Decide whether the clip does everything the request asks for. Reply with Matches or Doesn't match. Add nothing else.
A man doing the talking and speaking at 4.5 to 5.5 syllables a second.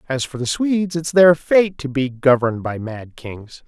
Matches